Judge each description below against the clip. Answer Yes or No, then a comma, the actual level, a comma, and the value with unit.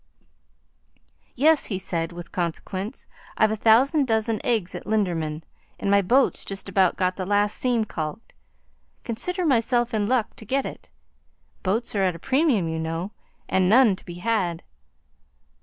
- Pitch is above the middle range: Yes, high, 205 Hz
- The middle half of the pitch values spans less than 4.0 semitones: No, average, 4.7 semitones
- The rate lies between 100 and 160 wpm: Yes, average, 155 wpm